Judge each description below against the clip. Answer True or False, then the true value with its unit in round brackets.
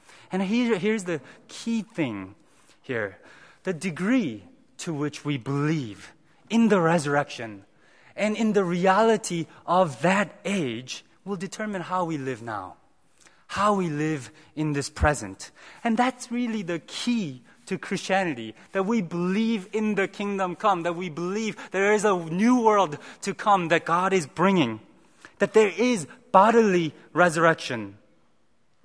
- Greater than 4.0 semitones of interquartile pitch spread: True (5.2 semitones)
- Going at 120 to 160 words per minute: True (140 wpm)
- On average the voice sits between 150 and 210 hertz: True (185 Hz)